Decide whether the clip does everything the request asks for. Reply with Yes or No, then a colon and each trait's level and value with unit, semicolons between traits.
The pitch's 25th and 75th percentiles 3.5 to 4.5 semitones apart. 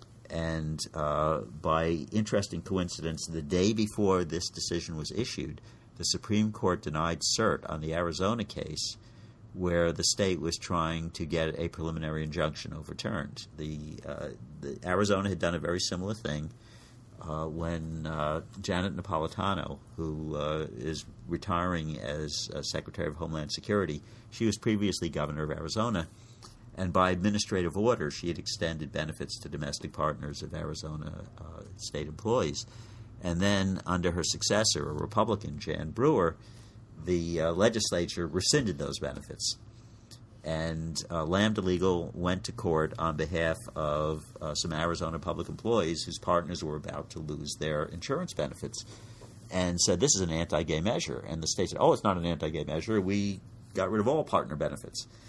No: average, 4.9 semitones